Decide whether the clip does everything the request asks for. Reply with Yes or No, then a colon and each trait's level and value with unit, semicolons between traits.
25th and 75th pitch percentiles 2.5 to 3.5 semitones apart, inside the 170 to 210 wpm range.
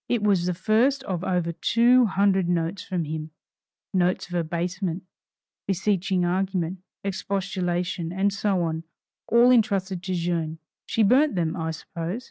No: average, 2.8 semitones; average, 140 wpm